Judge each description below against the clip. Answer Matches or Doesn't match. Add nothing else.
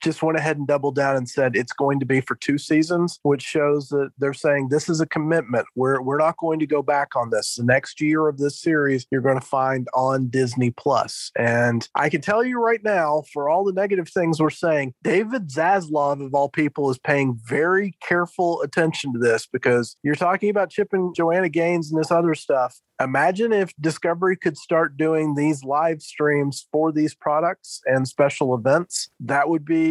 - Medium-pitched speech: Matches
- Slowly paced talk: Doesn't match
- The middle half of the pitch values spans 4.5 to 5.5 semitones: Doesn't match